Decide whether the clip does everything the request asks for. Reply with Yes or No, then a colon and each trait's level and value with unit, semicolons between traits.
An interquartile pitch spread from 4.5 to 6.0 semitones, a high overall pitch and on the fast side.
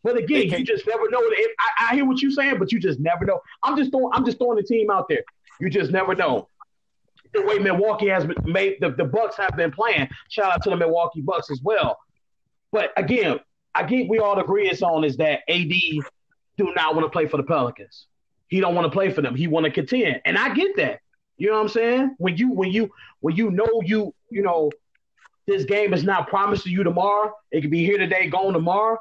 Yes: average, 5.2 semitones; high, 200 Hz; fast, 240 wpm